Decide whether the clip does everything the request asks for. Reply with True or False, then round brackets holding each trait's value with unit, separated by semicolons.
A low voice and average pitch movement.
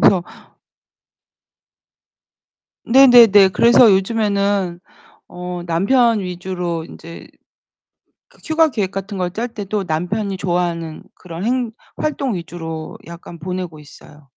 False (190 Hz; 4.0 semitones)